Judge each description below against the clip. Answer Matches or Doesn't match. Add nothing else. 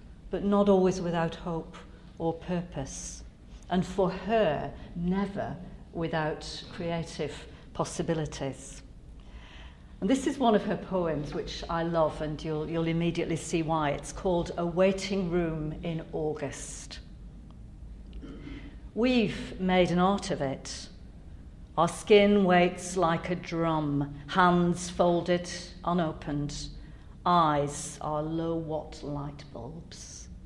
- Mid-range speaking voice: Matches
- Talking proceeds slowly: Matches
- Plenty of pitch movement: Doesn't match